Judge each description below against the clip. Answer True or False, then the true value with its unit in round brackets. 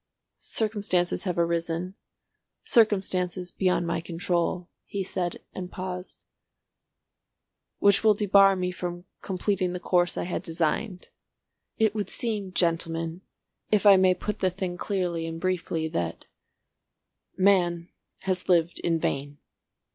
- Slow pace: True (115 wpm)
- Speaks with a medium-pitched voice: True (180 Hz)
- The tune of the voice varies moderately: False (2.2 semitones)